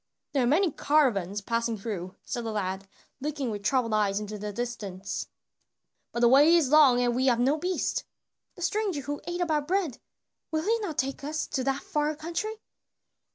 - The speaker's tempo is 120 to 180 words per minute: No, average, 190 wpm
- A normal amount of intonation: No, wide, 5.7 semitones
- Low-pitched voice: No, very high, 265 Hz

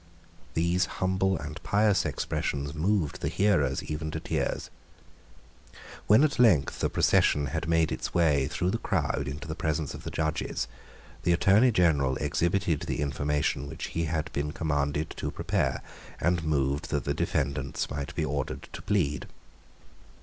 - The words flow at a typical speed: Yes, average, 155 wpm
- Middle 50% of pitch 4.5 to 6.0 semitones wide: No, average, 3.7 semitones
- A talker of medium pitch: No, very low, 80 Hz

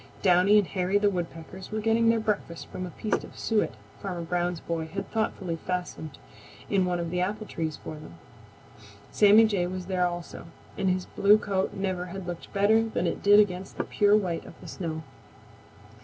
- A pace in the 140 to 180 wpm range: No, average, 190 wpm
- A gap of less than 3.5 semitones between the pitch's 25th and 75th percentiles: Yes, average, 2.8 semitones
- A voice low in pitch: No, medium, 185 Hz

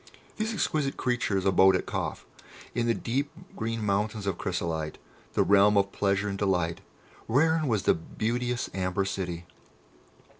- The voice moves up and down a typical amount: Yes, average, 4.0 semitones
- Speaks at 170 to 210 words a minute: No, average, 145 wpm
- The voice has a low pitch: Yes, low, 100 Hz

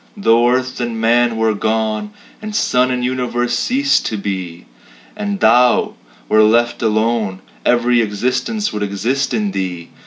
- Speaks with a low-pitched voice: Yes, low, 120 Hz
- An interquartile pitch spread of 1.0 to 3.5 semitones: Yes, average, 2.7 semitones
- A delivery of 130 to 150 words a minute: Yes, average, 145 wpm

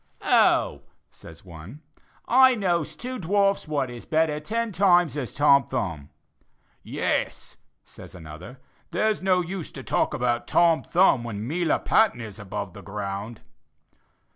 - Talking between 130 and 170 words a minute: Yes, average, 140 wpm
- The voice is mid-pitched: Yes, medium, 145 Hz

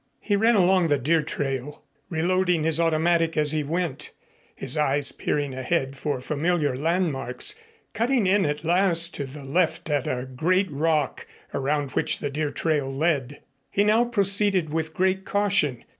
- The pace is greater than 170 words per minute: No, average, 160 wpm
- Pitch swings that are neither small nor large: Yes, average, 4.4 semitones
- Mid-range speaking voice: Yes, medium, 160 Hz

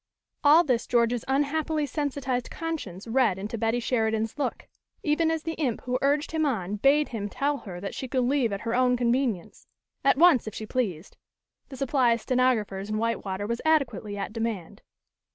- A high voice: Yes, high, 245 Hz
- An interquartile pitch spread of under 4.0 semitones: No, average, 4.6 semitones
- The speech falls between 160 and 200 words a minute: Yes, average, 180 wpm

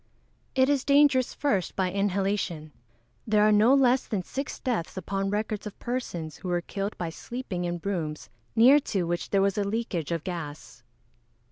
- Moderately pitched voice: No, high, 200 Hz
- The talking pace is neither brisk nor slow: Yes, average, 175 wpm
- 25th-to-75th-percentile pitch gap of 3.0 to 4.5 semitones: No, wide, 5.4 semitones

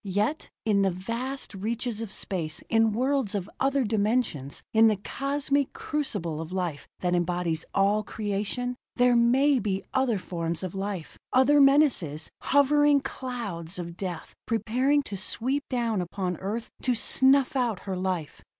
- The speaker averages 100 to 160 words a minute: Yes, average, 150 wpm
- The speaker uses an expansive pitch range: Yes, wide, 5.9 semitones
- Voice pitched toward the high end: Yes, high, 215 Hz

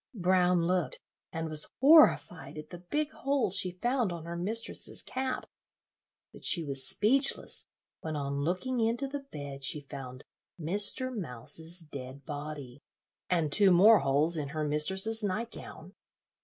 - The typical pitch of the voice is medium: Yes, medium, 175 Hz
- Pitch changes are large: Yes, wide, 7.0 semitones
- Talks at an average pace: Yes, average, 145 wpm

